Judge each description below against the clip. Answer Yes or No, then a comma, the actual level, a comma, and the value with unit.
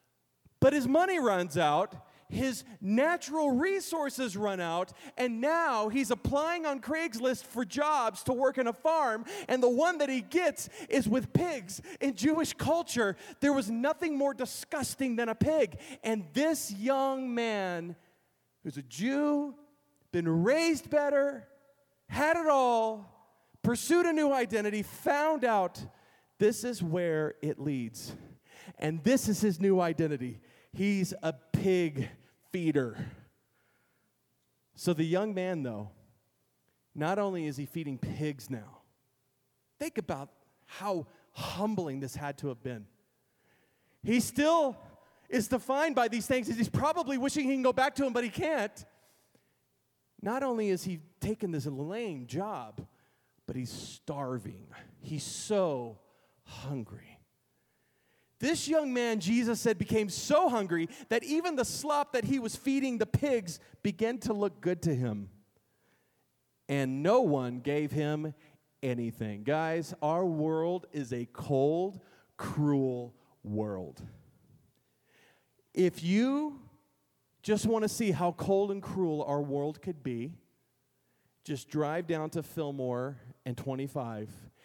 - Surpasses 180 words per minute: No, slow, 135 wpm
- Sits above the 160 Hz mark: Yes, high, 190 Hz